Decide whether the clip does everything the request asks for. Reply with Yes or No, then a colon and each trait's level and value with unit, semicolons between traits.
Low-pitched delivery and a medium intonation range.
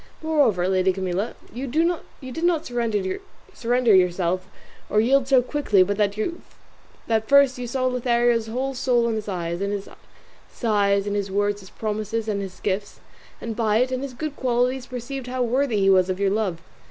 No: high, 225 Hz; average, 4.2 semitones